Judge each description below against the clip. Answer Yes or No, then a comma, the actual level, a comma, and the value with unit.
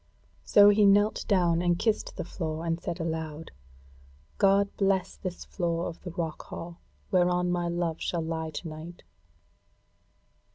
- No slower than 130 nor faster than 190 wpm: Yes, average, 150 wpm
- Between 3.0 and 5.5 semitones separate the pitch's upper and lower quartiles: No, narrow, 2.5 semitones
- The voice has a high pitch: No, medium, 175 Hz